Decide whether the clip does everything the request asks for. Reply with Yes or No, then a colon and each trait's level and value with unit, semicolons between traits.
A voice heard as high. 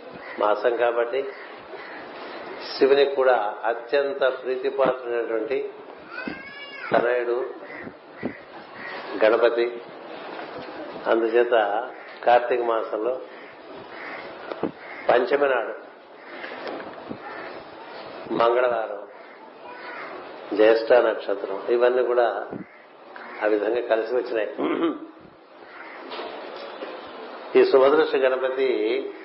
No: low, 125 Hz